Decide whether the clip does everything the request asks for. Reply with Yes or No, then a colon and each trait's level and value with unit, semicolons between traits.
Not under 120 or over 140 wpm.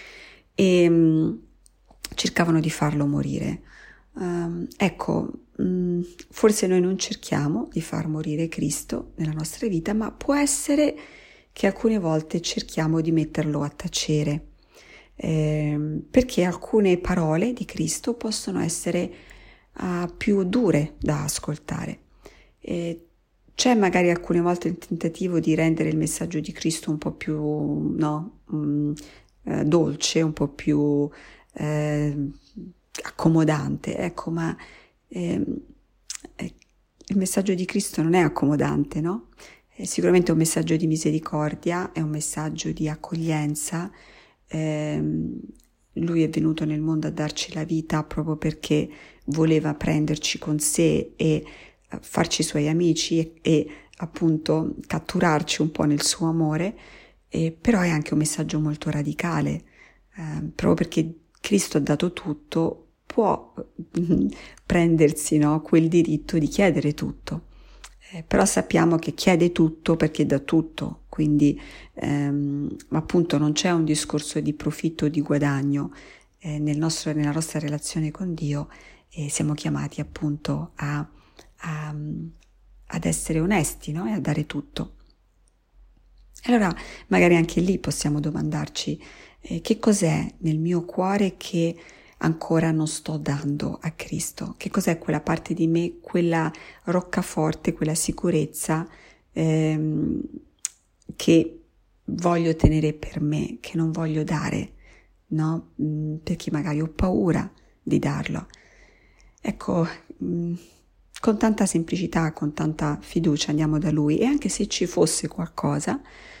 Yes: average, 125 wpm